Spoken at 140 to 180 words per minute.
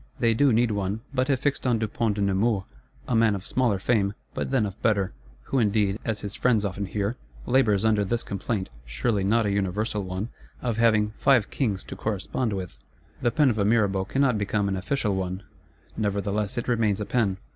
No: average, 195 wpm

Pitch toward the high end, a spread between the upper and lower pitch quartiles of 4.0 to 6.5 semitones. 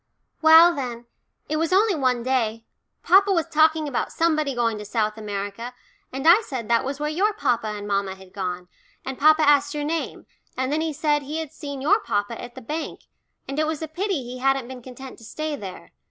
Yes: very high, 270 Hz; average, 5.2 semitones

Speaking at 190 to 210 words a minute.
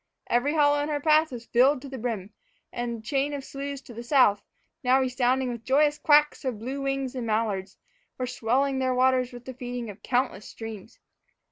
Yes: average, 200 wpm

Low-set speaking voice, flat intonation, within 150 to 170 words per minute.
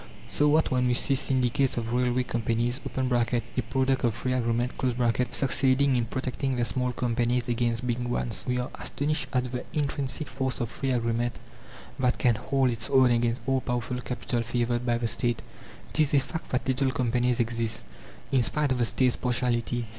No: low, 125 Hz; narrow, 1.8 semitones; average, 180 wpm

